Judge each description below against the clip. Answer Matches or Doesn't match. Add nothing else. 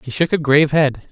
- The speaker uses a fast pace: Matches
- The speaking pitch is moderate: Matches